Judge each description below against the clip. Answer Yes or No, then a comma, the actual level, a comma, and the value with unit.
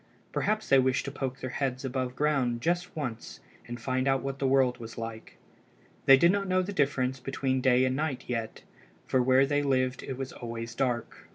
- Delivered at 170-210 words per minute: Yes, average, 200 wpm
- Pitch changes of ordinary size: No, narrow, 1.7 semitones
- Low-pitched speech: Yes, low, 130 Hz